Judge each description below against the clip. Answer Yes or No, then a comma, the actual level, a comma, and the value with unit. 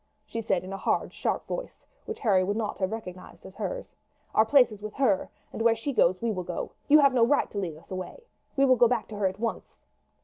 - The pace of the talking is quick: Yes, fast, 250 wpm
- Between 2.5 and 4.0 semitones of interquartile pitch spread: No, average, 5.1 semitones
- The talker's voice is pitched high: Yes, high, 220 Hz